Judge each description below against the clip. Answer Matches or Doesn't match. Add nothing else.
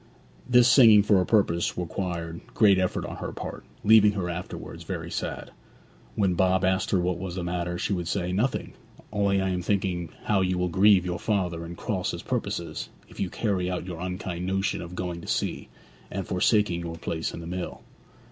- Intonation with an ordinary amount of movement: Doesn't match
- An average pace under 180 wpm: Doesn't match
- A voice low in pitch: Matches